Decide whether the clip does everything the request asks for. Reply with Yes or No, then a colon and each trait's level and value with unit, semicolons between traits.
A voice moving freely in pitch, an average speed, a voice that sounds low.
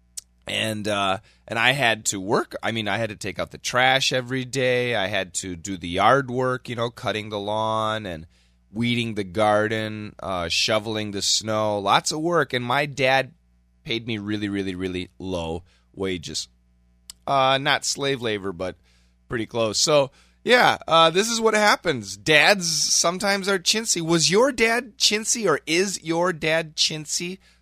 Yes: wide, 8.2 semitones; average, 170 wpm; low, 110 Hz